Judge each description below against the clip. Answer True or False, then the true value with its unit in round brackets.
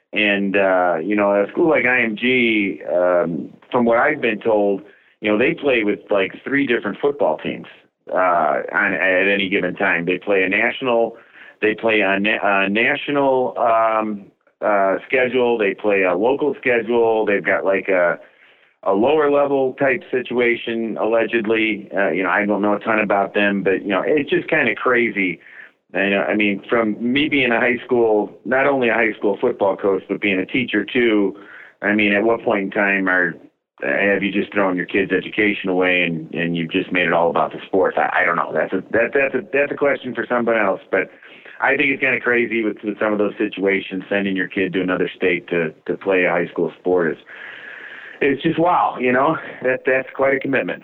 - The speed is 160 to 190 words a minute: False (205 wpm)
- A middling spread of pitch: True (3.8 semitones)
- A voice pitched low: True (105 Hz)